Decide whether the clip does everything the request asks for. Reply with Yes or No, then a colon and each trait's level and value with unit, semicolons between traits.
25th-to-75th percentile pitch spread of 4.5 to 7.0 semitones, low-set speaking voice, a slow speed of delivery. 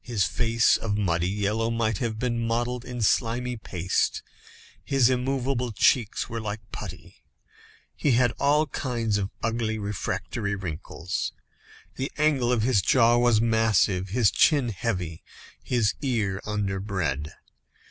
No: average, 3.4 semitones; low, 115 Hz; slow, 130 wpm